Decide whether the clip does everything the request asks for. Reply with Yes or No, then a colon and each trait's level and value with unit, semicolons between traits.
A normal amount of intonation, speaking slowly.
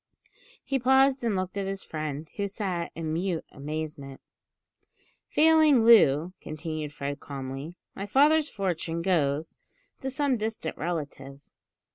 No: wide, 6.9 semitones; slow, 125 wpm